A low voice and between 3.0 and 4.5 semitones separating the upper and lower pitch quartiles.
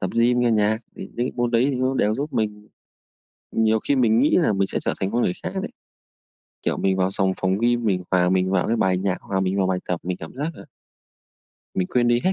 Yes: low, 105 Hz; average, 4.2 semitones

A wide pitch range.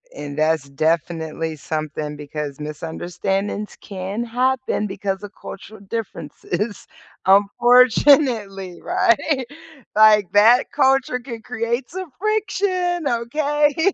Yes: wide, 7.6 semitones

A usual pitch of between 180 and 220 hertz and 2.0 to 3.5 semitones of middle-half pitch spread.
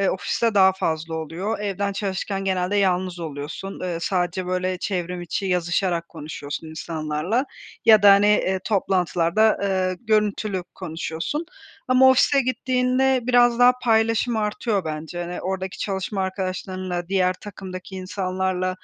Yes: high, 190 Hz; average, 2.8 semitones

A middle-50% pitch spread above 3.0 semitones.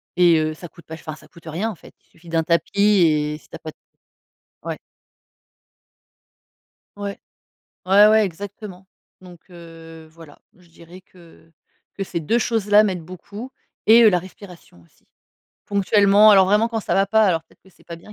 Yes: average, 3.7 semitones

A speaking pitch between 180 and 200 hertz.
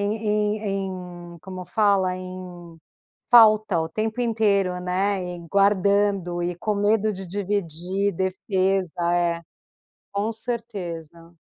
Yes: high, 190 Hz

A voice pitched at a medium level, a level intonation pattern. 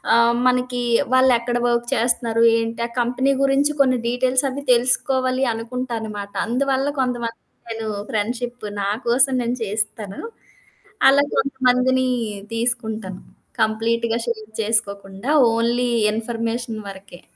No: high, 235 Hz; narrow, 2.2 semitones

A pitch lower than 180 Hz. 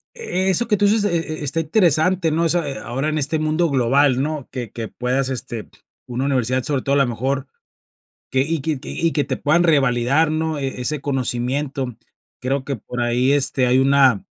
Yes: medium, 140 Hz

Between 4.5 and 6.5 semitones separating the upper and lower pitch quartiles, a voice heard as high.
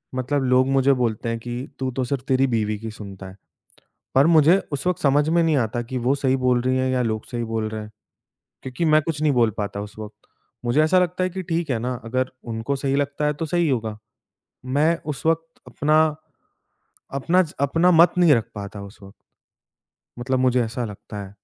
No: average, 4.9 semitones; low, 130 Hz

